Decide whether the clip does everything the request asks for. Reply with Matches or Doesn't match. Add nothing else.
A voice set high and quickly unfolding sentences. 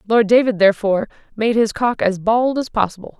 Doesn't match